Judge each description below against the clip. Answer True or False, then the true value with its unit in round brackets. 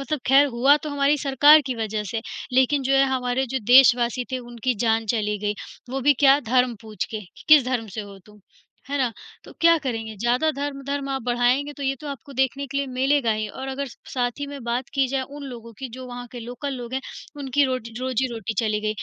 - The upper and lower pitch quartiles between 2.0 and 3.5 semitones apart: True (2.7 semitones)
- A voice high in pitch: True (255 Hz)